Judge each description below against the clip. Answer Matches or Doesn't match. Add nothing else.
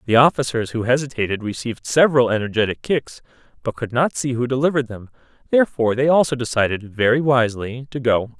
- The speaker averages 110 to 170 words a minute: Matches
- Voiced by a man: Matches